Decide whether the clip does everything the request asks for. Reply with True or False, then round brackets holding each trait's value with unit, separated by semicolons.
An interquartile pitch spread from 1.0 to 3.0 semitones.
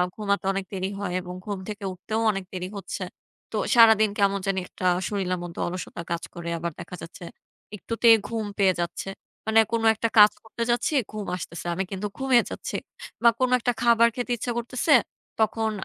False (3.7 semitones)